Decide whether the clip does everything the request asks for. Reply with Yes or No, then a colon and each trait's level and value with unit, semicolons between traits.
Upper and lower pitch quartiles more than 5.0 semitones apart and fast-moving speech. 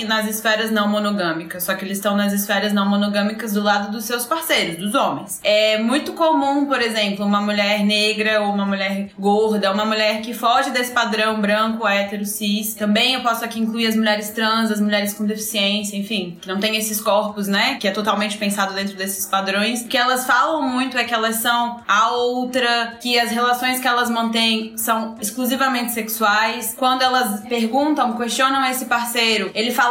No: narrow, 2.6 semitones; fast, 190 wpm